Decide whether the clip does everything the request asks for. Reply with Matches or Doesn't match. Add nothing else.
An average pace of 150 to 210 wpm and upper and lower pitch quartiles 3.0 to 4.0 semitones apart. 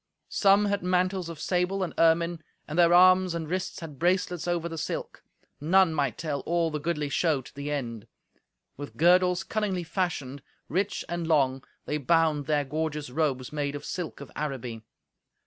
Matches